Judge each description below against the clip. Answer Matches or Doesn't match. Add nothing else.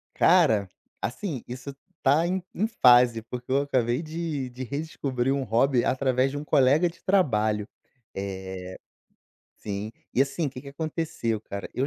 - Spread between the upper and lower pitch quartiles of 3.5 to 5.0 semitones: Matches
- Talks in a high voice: Doesn't match